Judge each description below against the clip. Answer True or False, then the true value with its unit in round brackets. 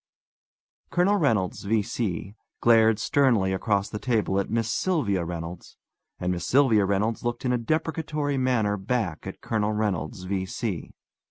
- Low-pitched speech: True (110 Hz)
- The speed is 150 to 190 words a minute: False (140 wpm)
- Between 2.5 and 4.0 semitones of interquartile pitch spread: False (4.5 semitones)